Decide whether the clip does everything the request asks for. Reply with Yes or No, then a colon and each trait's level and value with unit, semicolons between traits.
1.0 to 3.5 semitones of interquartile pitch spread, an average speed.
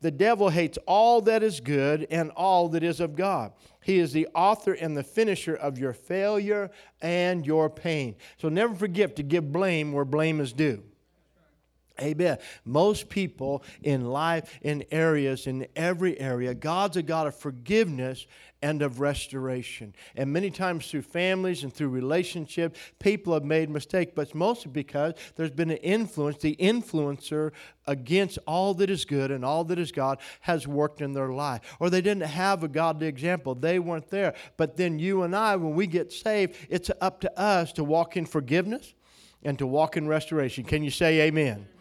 No: average, 4.2 semitones; average, 180 wpm